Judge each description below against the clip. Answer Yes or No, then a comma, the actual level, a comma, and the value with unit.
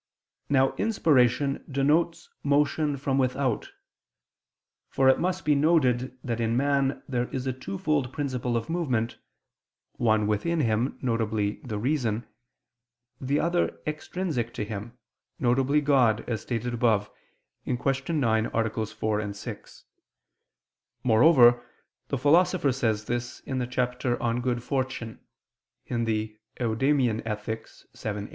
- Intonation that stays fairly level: No, average, 3.7 semitones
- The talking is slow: Yes, slow, 115 wpm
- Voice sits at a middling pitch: No, low, 125 Hz